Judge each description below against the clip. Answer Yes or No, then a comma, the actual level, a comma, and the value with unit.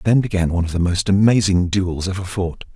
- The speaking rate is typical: No, fast, 220 wpm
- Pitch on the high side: No, very low, 95 Hz